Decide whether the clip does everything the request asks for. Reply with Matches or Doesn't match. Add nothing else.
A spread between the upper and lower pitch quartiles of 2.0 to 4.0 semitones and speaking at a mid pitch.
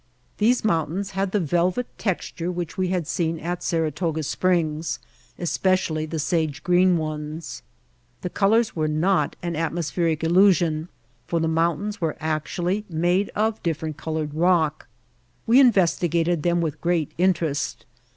Matches